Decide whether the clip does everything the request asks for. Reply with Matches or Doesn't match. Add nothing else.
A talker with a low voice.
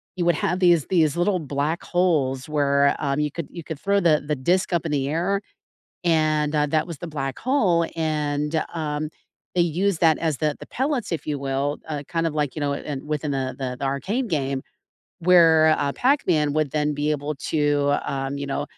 Doesn't match